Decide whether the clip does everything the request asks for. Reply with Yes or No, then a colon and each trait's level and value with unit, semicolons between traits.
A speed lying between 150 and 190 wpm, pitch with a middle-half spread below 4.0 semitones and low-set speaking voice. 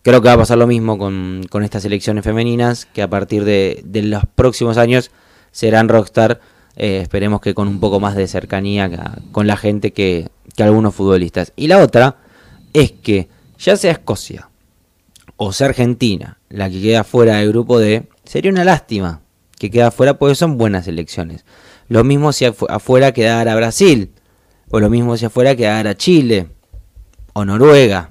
Yes: average, 175 wpm; average, 3.3 semitones; low, 105 Hz